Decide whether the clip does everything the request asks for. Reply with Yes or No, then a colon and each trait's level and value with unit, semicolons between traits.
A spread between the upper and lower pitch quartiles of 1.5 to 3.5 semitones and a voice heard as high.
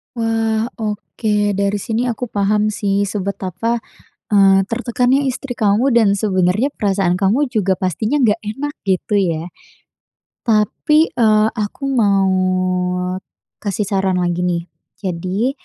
Yes: average, 3.1 semitones; high, 210 Hz